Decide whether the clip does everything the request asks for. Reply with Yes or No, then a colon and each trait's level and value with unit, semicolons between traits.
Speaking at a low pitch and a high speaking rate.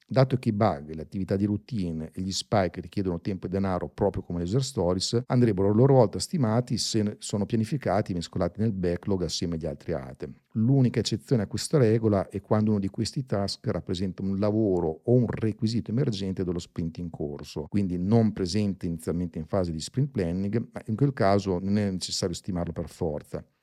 Yes: low, 100 Hz; fast, 195 wpm